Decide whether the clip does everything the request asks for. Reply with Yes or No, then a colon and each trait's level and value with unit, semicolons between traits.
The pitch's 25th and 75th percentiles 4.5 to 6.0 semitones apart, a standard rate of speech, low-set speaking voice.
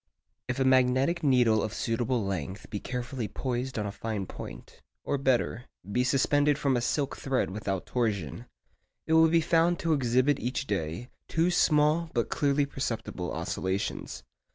Yes: average, 4.8 semitones; average, 150 wpm; low, 125 Hz